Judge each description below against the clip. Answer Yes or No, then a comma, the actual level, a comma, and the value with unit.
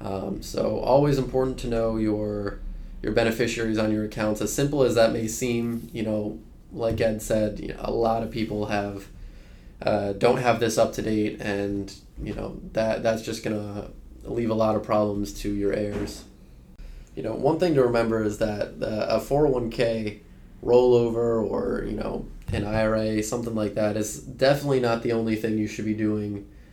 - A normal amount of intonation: No, narrow, 1.9 semitones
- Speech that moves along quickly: No, average, 185 wpm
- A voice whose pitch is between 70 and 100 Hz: No, low, 110 Hz